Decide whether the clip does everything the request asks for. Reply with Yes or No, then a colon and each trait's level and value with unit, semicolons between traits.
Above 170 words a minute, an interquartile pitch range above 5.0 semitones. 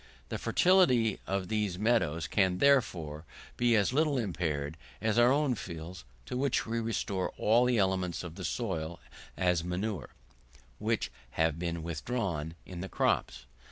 No: average, 150 wpm; wide, 5.6 semitones